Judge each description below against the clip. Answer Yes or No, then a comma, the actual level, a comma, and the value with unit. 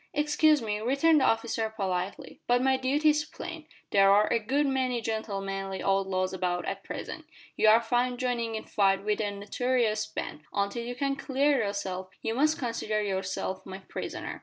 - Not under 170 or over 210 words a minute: Yes, average, 175 wpm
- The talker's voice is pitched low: No, high, 225 Hz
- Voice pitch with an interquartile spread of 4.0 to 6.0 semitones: Yes, average, 4.9 semitones